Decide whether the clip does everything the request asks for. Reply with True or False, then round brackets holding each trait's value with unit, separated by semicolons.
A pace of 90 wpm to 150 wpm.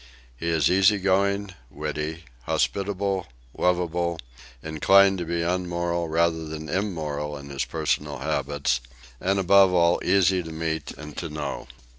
True (135 wpm)